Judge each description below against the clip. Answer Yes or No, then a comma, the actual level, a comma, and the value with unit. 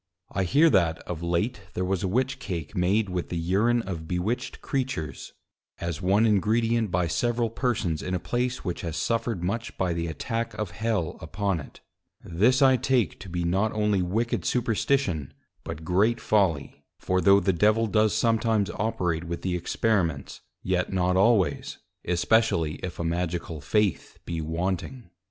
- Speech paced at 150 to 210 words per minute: Yes, average, 165 wpm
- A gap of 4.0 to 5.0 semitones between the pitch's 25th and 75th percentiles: Yes, average, 4.7 semitones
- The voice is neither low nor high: No, very low, 95 Hz